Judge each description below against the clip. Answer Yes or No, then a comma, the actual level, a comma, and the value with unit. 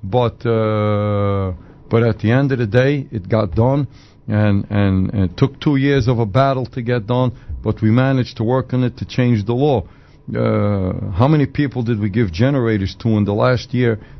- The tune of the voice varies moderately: Yes, average, 3.5 semitones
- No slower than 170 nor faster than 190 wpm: No, fast, 205 wpm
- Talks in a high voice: No, low, 115 Hz